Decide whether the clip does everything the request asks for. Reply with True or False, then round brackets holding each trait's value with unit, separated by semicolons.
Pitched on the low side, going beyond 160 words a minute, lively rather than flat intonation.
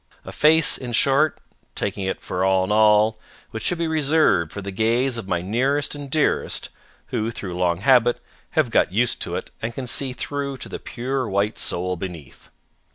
True (115 Hz; 190 wpm; 6.0 semitones)